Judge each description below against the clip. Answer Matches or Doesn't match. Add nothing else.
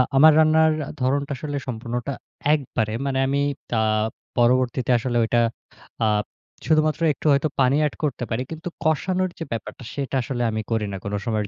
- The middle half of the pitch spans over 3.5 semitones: Matches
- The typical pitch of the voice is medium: Doesn't match